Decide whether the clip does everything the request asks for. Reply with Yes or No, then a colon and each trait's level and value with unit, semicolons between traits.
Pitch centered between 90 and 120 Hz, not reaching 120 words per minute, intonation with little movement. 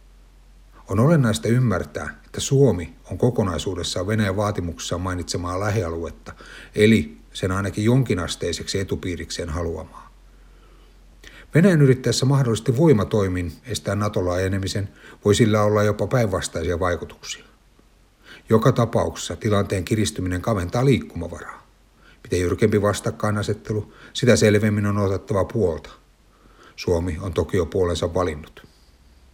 No: low, 105 Hz; average, 100 wpm; average, 3.8 semitones